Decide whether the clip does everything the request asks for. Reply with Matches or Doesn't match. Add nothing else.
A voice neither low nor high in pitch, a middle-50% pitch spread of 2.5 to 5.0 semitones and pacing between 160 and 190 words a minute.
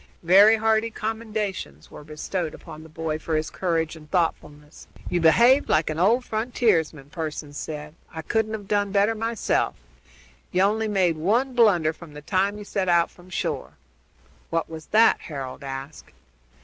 Doesn't match